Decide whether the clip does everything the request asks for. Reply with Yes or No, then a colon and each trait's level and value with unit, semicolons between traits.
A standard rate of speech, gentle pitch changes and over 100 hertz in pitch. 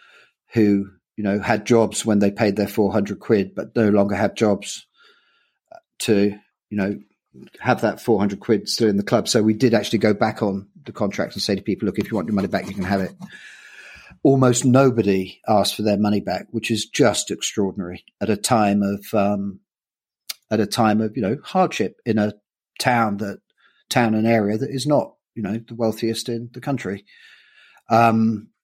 Yes: average, 195 wpm; narrow, 2.1 semitones; low, 110 Hz